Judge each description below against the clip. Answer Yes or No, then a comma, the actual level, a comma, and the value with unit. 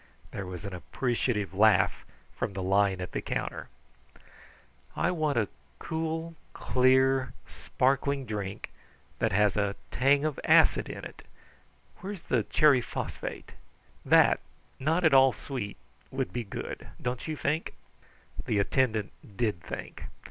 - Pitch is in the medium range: No, low, 125 Hz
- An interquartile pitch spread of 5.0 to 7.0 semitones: Yes, wide, 5.6 semitones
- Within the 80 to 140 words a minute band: Yes, slow, 135 wpm